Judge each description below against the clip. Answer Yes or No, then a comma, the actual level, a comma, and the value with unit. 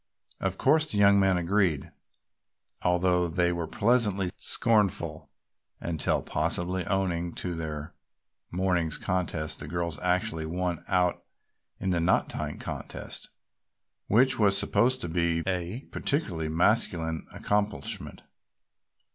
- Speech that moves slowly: Yes, slow, 115 wpm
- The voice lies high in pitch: No, very low, 90 Hz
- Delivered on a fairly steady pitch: No, average, 3.0 semitones